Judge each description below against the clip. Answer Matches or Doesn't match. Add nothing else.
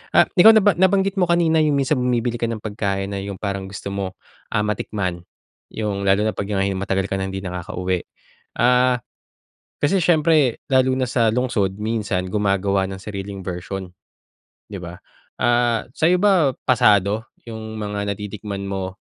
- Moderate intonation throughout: Matches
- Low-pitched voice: Matches